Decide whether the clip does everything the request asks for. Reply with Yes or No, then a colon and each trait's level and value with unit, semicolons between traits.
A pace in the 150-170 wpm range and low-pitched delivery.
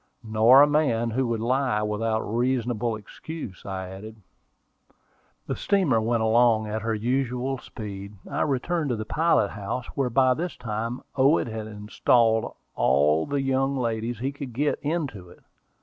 Yes: average, 160 wpm; low, 115 Hz